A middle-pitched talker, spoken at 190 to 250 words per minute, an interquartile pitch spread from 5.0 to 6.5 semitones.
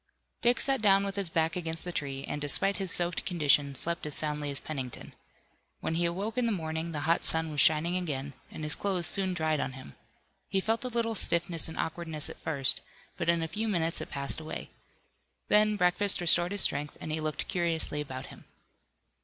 No: medium, 165 Hz; fast, 205 wpm; average, 3.9 semitones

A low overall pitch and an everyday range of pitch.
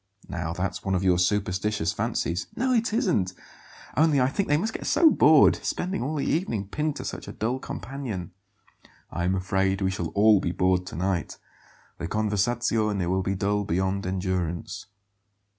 No: low, 100 Hz; wide, 6.2 semitones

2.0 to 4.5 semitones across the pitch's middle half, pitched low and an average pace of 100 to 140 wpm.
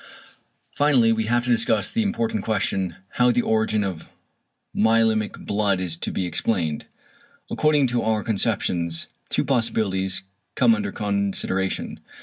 Yes: average, 4.1 semitones; low, 110 Hz; slow, 135 wpm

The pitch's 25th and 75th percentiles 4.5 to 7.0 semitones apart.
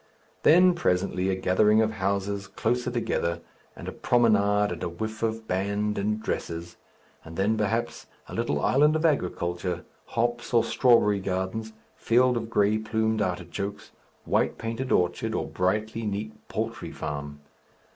No: average, 3.4 semitones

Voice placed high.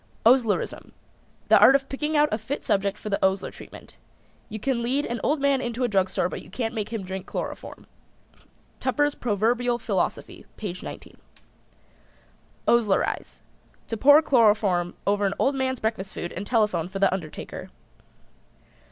Yes: high, 225 Hz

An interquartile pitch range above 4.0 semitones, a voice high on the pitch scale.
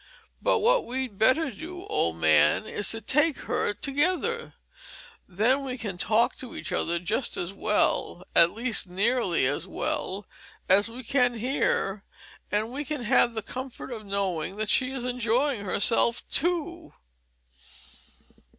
Yes: average, 5.3 semitones; high, 235 Hz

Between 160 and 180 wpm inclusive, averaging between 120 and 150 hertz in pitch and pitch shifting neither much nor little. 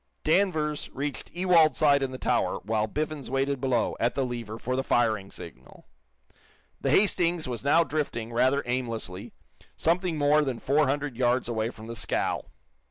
Yes: average, 165 wpm; low, 135 Hz; average, 4.4 semitones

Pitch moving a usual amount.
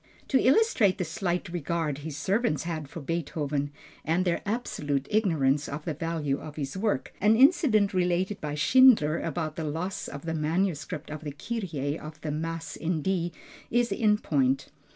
Yes: average, 4.5 semitones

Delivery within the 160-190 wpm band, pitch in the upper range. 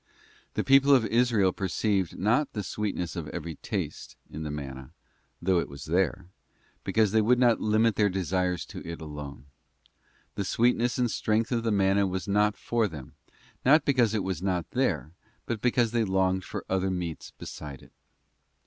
No: average, 175 wpm; very low, 95 Hz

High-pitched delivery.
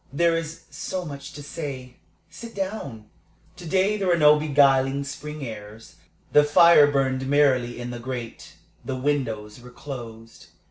No: medium, 140 Hz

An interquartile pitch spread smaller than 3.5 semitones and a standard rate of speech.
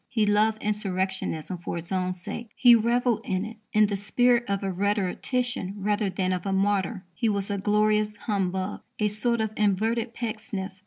Yes: narrow, 2.5 semitones; average, 175 wpm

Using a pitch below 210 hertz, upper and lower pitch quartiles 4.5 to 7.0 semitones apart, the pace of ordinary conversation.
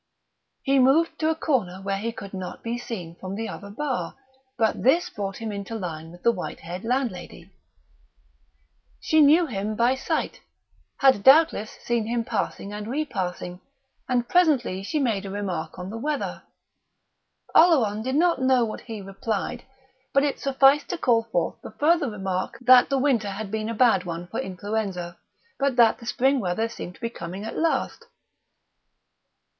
No: high, 225 Hz; wide, 5.4 semitones; average, 170 wpm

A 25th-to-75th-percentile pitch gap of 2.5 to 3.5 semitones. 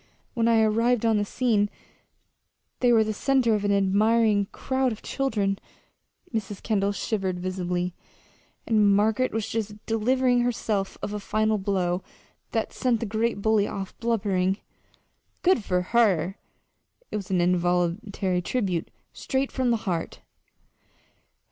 Yes: average, 3.1 semitones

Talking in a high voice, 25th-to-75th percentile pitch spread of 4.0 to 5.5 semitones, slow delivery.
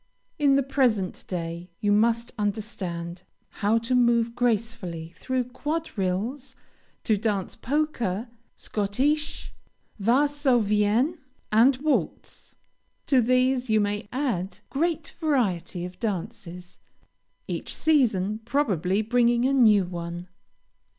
Yes: high, 225 Hz; average, 5.0 semitones; slow, 105 wpm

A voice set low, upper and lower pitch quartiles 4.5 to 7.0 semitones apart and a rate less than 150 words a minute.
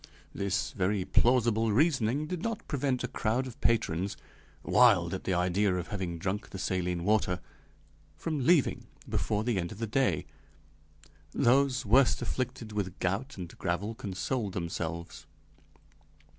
Yes: low, 105 Hz; wide, 5.5 semitones; average, 140 wpm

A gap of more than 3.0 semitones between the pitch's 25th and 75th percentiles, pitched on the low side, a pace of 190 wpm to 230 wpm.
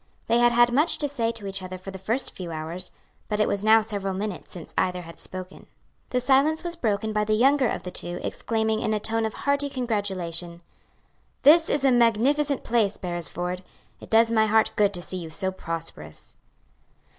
No: average, 4.6 semitones; high, 215 Hz; average, 200 wpm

